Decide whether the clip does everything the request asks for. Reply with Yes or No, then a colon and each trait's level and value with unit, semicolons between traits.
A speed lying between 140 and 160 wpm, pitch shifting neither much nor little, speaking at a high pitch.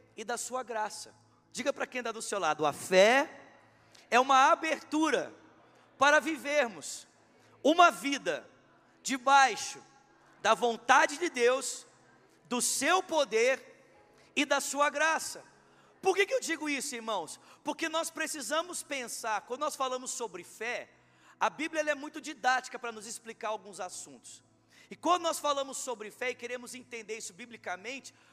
Yes: average, 150 wpm; average, 4.3 semitones; very high, 265 Hz